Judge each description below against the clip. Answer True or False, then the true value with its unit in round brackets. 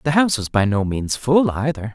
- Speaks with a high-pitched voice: False (125 Hz)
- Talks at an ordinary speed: False (245 wpm)